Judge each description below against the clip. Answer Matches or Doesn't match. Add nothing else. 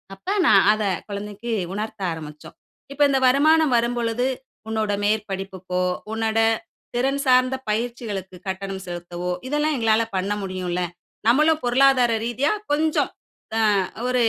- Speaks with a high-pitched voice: Matches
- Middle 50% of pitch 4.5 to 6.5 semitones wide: Matches